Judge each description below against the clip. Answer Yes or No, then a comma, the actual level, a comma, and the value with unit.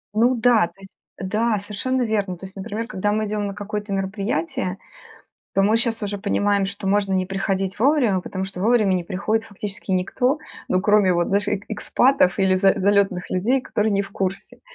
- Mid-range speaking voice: No, high, 200 Hz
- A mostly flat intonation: Yes, narrow, 2.2 semitones